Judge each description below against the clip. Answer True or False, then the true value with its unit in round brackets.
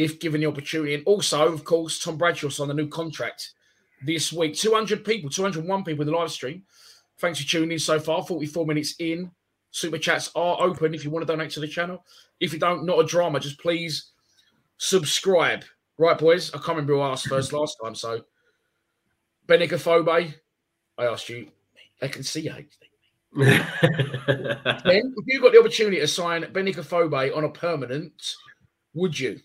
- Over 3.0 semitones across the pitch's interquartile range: False (2.7 semitones)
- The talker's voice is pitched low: False (165 Hz)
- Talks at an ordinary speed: True (175 wpm)